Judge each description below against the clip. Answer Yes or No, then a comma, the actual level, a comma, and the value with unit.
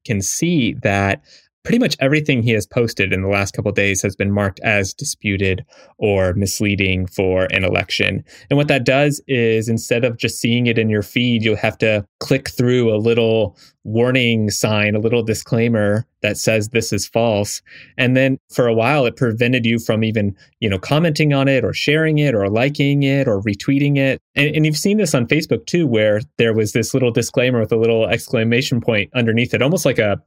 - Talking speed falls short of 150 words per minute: No, fast, 205 wpm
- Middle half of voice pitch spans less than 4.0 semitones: No, average, 4.3 semitones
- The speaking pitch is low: Yes, low, 115 Hz